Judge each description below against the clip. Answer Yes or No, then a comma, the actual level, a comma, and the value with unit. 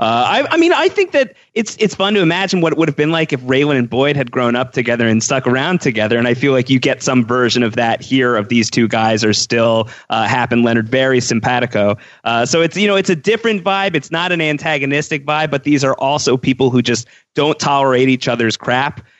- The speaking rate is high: Yes, fast, 245 wpm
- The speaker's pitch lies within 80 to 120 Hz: No, low, 135 Hz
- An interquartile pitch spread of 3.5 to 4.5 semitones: No, average, 5.3 semitones